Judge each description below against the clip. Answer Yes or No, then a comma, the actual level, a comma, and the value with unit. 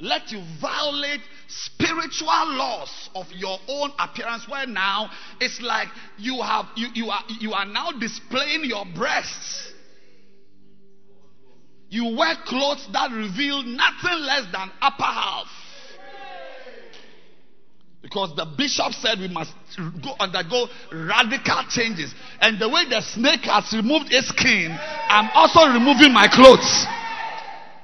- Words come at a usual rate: No, slow, 125 wpm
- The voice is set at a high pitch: Yes, high, 230 Hz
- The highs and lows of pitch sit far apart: Yes, wide, 6.5 semitones